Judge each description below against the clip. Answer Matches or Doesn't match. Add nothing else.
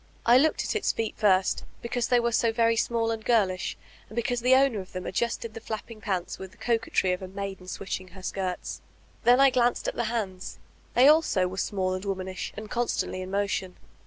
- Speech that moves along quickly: Matches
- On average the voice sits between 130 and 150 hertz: Doesn't match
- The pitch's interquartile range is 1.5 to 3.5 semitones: Doesn't match